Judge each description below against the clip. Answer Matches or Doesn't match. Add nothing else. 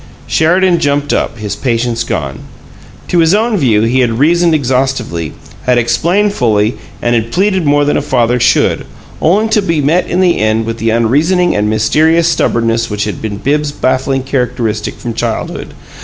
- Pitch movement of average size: Doesn't match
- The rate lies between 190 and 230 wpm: Doesn't match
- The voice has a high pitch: Doesn't match